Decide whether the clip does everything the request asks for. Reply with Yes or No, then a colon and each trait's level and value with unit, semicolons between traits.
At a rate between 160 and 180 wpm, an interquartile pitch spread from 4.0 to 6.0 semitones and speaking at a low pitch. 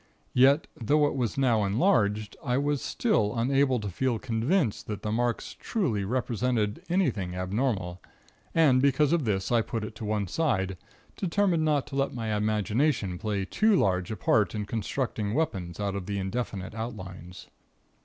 Yes: average, 165 wpm; average, 5.2 semitones; low, 115 Hz